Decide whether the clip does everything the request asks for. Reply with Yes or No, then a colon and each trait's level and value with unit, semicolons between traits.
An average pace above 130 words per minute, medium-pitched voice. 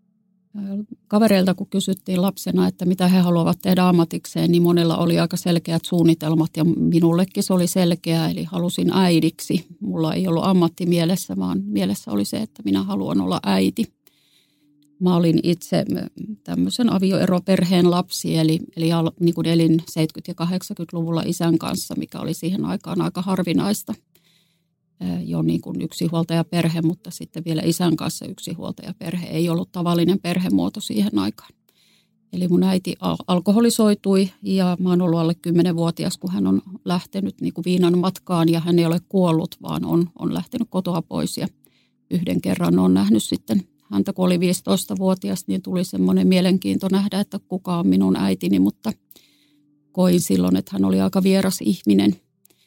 Yes: fast, 155 wpm; medium, 175 Hz